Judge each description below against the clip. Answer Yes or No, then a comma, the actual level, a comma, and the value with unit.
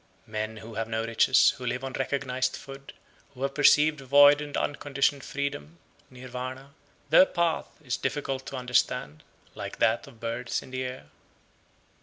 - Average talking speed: Yes, average, 160 wpm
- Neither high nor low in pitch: No, low, 130 Hz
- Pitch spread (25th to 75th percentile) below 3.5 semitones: Yes, average, 3.0 semitones